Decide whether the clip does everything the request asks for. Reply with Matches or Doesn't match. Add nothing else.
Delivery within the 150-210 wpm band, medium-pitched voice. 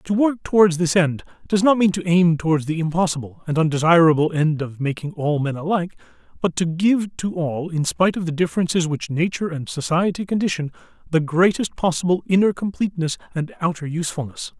Matches